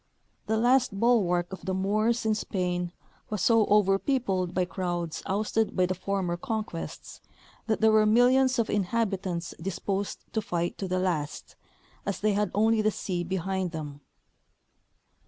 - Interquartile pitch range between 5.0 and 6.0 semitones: No, average, 3.4 semitones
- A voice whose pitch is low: No, high, 195 Hz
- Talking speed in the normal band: Yes, average, 155 wpm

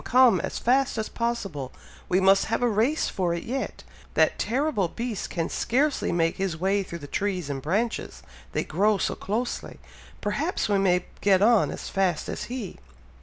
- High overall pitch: Yes, high, 205 Hz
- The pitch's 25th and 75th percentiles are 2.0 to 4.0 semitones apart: No, average, 4.7 semitones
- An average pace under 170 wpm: No, average, 175 wpm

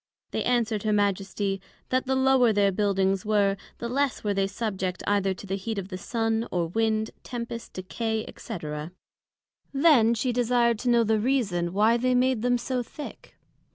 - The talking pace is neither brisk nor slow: Yes, average, 175 wpm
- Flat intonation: No, average, 3.7 semitones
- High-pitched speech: Yes, high, 220 Hz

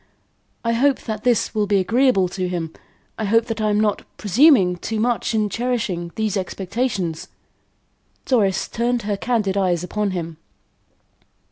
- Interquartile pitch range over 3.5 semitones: Yes, average, 3.9 semitones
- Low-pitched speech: No, high, 210 Hz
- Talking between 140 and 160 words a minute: Yes, average, 150 wpm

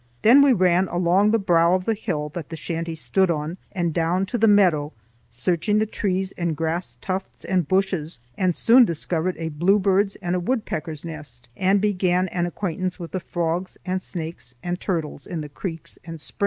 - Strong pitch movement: No, average, 2.8 semitones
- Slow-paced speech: No, average, 190 wpm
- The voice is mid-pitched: Yes, medium, 175 Hz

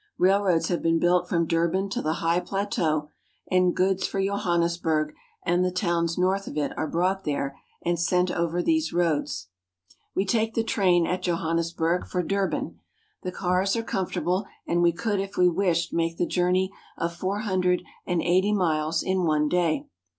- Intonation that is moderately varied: No, narrow, 2.1 semitones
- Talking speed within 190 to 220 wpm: No, average, 170 wpm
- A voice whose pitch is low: No, medium, 180 Hz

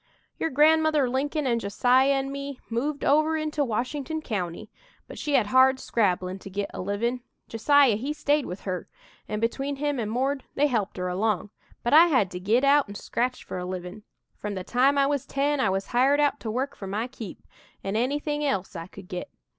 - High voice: Yes, very high, 255 Hz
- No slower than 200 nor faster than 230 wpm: Yes, fast, 205 wpm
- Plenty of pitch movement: Yes, wide, 5.9 semitones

